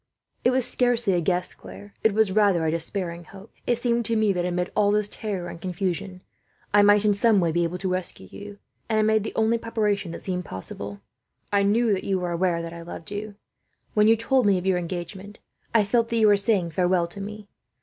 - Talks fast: Yes, fast, 230 wpm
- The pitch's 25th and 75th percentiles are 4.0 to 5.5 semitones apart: No, average, 3.5 semitones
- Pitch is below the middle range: No, high, 200 Hz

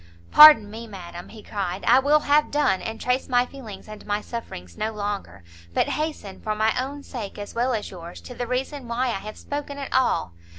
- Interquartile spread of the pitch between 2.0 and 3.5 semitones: No, average, 4.5 semitones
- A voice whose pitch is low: No, high, 230 Hz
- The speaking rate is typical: No, fast, 210 wpm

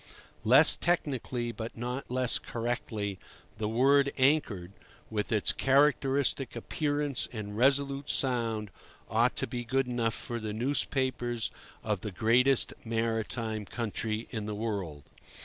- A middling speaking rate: No, slow, 125 wpm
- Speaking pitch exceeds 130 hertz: No, low, 120 Hz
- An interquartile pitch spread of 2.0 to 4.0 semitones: Yes, average, 3.6 semitones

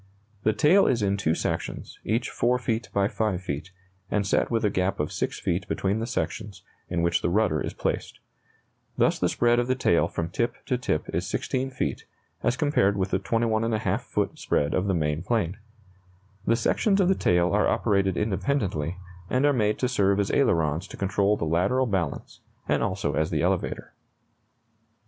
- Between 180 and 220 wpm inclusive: Yes, average, 185 wpm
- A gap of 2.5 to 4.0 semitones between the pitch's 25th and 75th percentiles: No, average, 5.1 semitones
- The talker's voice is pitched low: Yes, low, 100 Hz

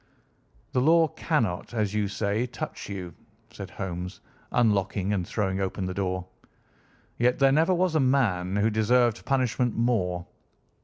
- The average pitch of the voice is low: Yes, low, 105 Hz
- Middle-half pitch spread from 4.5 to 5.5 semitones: Yes, average, 4.8 semitones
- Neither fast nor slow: Yes, average, 145 wpm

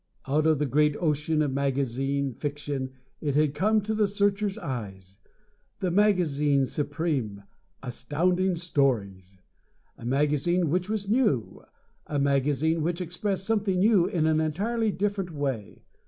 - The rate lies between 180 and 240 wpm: No, slow, 135 wpm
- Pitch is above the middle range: No, medium, 150 Hz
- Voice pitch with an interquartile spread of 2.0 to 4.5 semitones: No, average, 5.2 semitones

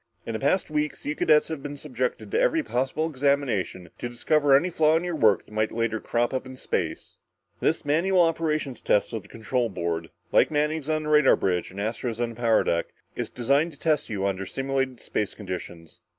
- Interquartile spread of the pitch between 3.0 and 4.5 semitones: No, wide, 5.5 semitones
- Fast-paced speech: Yes, fast, 210 wpm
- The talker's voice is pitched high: No, low, 135 Hz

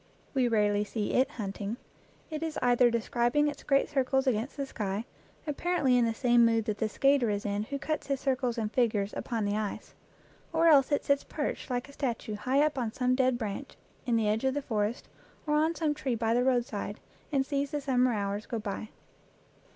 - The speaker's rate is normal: No, fast, 210 wpm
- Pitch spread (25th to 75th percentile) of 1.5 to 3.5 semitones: No, average, 4.2 semitones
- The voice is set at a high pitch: Yes, high, 245 Hz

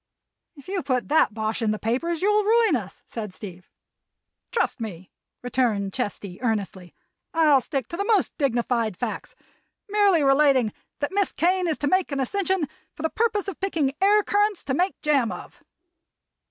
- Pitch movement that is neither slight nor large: No, wide, 8.9 semitones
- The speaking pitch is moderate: No, very high, 285 Hz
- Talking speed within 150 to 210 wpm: Yes, average, 165 wpm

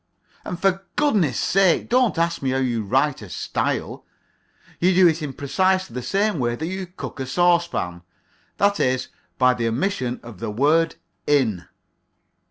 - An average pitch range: No, wide, 6.7 semitones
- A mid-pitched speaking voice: Yes, medium, 150 Hz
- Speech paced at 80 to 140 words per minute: No, average, 165 wpm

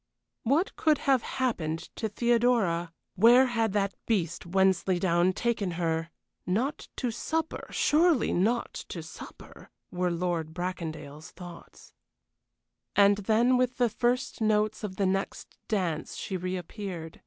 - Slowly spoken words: Yes, slow, 125 wpm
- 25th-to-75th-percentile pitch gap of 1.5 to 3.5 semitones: No, wide, 5.4 semitones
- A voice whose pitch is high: Yes, high, 195 Hz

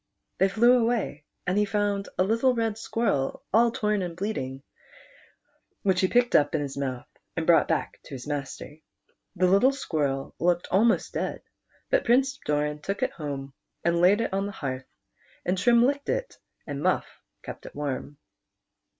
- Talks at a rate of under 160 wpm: No, average, 170 wpm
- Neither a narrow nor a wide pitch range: No, wide, 7.4 semitones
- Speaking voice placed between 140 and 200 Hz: Yes, medium, 185 Hz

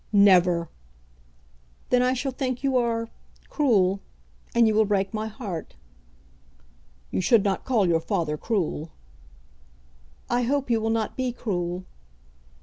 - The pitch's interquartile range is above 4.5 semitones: Yes, average, 5.0 semitones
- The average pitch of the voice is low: No, high, 220 Hz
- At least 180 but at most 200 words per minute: No, slow, 135 wpm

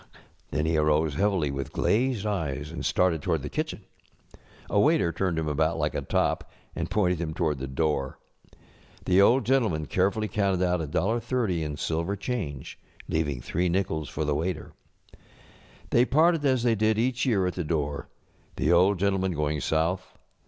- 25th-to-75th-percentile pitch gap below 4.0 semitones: No, average, 5.0 semitones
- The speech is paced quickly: No, average, 170 wpm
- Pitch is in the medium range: No, very low, 85 Hz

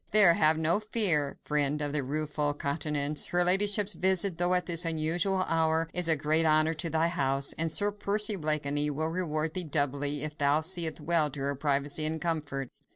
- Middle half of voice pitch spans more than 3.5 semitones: No, average, 3.1 semitones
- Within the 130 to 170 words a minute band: No, average, 190 wpm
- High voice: No, medium, 160 Hz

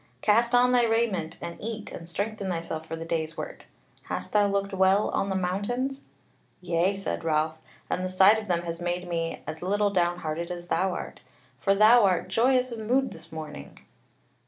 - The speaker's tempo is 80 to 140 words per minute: No, average, 185 wpm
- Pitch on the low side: No, high, 190 Hz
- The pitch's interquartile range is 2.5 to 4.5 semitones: Yes, average, 4.1 semitones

